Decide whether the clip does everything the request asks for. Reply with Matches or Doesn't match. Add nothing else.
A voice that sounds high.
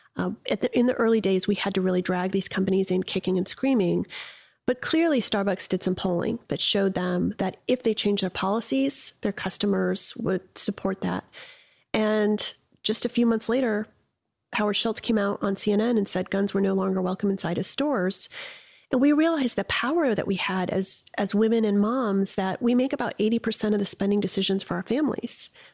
Matches